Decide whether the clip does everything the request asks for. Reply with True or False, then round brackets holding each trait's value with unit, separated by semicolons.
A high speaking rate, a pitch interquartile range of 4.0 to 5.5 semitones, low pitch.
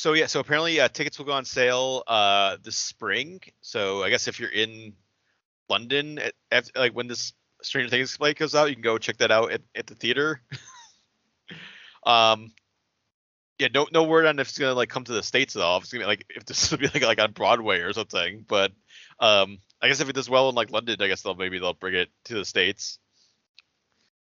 True (225 wpm; 4.7 semitones; 125 Hz)